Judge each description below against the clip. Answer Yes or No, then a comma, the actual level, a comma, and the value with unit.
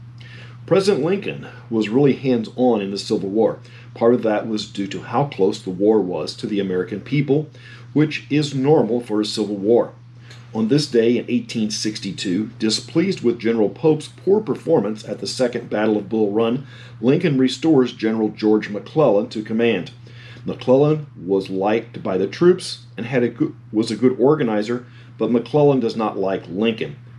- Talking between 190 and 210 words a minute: No, average, 170 wpm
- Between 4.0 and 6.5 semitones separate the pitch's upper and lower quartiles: No, average, 2.9 semitones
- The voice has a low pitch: Yes, low, 120 Hz